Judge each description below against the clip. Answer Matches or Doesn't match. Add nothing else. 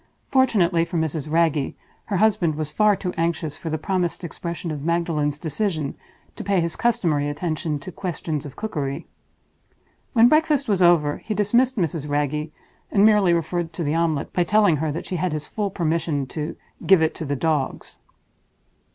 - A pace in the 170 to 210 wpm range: Matches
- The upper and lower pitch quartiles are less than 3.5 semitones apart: Doesn't match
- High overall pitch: Doesn't match